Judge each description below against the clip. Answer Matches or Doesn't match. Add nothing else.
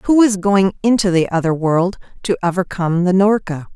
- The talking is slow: Doesn't match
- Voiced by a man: Doesn't match